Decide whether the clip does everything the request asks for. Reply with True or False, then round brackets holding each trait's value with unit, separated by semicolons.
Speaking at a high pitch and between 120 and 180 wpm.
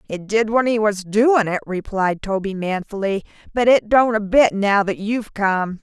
False (205 Hz; 195 wpm)